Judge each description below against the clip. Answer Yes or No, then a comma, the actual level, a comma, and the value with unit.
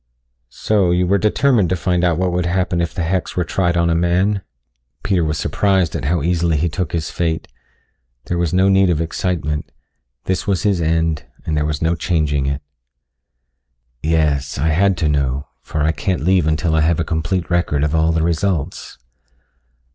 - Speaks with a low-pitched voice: Yes, very low, 85 Hz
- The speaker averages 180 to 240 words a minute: Yes, average, 190 wpm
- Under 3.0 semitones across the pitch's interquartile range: Yes, narrow, 2.6 semitones